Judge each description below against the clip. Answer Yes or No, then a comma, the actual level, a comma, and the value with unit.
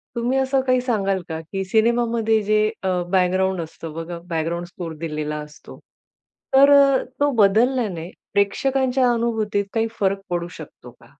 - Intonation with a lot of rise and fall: Yes, wide, 5.7 semitones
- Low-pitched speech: No, high, 205 Hz